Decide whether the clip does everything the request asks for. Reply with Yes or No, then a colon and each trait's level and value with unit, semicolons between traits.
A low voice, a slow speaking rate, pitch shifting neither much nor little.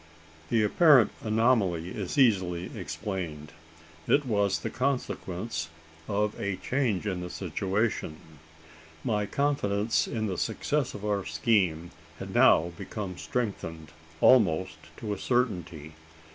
Yes: low, 100 Hz; slow, 120 wpm; average, 4.4 semitones